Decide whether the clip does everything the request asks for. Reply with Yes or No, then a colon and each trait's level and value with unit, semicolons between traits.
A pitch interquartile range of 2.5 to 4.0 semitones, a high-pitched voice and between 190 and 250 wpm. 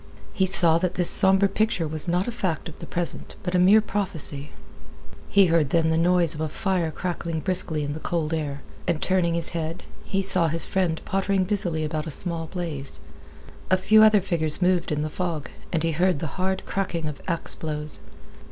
No: average, 2.9 semitones; medium, 170 Hz; average, 200 wpm